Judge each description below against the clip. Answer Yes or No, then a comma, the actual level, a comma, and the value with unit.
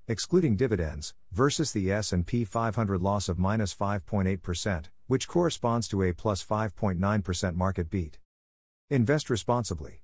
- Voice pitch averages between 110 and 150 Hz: No, low, 100 Hz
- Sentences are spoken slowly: Yes, slow, 120 wpm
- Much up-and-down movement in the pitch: No, average, 4.1 semitones